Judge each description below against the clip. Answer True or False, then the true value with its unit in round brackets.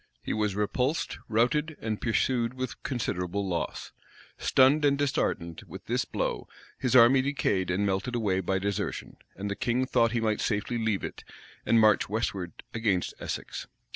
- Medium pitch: False (110 Hz)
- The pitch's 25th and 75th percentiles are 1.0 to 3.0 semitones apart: False (4.2 semitones)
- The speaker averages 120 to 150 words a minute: False (160 wpm)